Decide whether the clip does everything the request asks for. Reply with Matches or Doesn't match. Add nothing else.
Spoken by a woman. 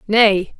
Matches